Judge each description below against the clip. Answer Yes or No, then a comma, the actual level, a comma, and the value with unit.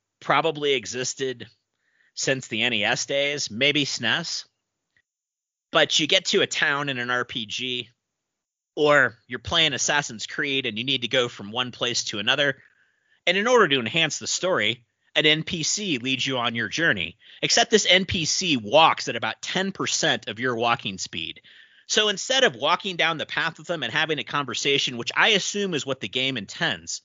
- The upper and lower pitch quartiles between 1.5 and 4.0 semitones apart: No, average, 4.9 semitones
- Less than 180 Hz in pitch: Yes, low, 135 Hz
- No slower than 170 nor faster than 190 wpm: Yes, average, 175 wpm